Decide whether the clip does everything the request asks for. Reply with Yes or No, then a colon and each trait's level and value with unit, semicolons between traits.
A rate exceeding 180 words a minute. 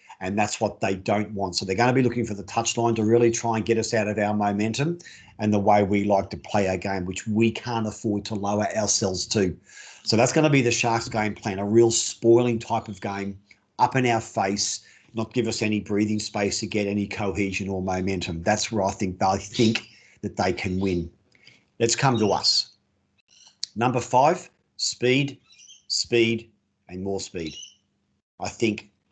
Yes: average, 195 wpm